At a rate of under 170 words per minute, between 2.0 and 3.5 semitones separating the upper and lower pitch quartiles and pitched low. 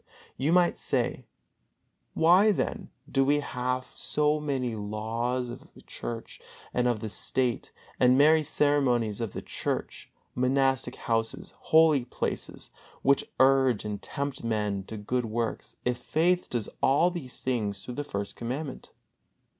No: slow, 135 wpm; average, 3.9 semitones; low, 125 Hz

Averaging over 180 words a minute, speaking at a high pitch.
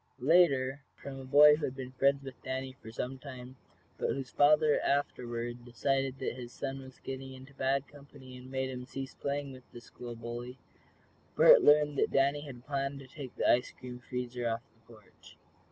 No: average, 190 wpm; low, 130 Hz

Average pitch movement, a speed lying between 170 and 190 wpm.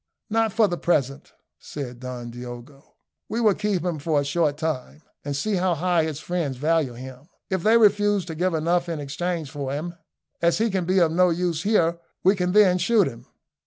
No: average, 4.5 semitones; average, 200 wpm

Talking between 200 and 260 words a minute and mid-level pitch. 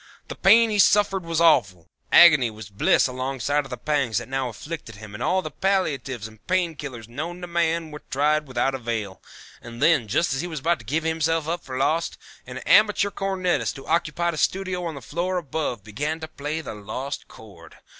Yes: fast, 205 wpm; medium, 150 Hz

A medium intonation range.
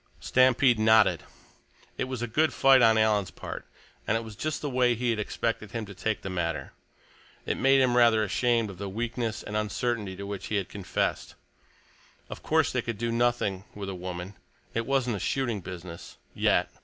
Yes: average, 3.4 semitones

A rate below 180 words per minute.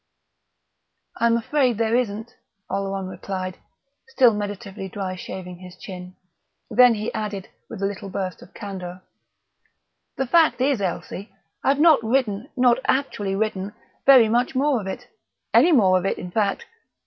Yes: average, 150 wpm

